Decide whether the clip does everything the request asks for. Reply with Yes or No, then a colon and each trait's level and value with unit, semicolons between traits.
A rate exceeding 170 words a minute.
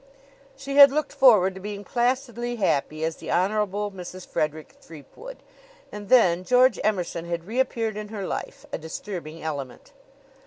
No: average, 150 wpm